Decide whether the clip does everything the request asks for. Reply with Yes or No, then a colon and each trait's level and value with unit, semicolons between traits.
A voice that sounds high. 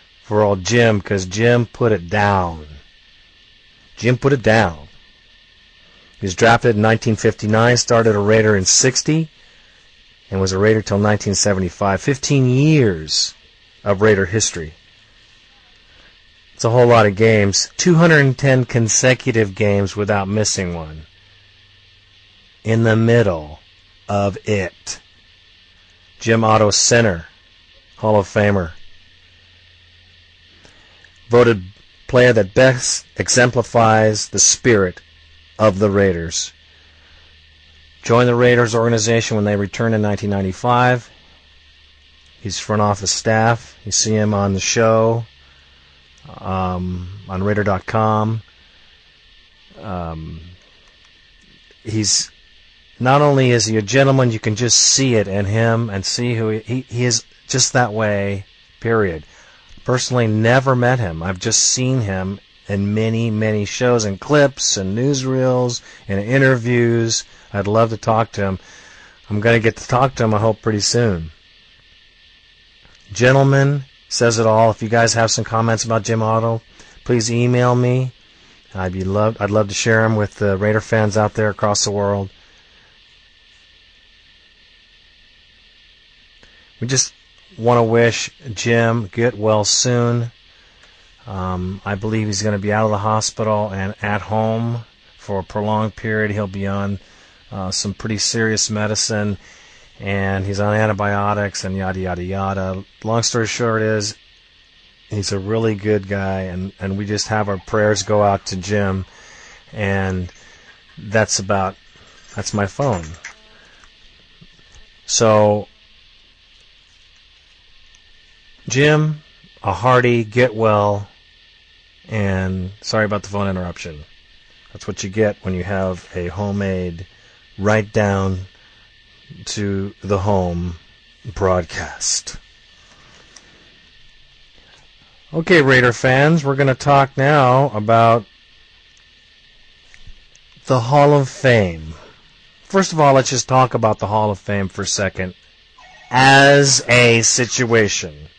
No: low, 105 Hz